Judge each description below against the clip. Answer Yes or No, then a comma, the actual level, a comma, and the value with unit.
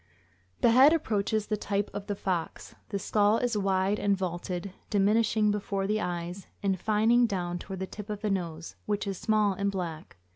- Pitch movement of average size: No, narrow, 2.2 semitones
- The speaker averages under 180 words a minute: No, average, 185 wpm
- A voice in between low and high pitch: No, high, 200 Hz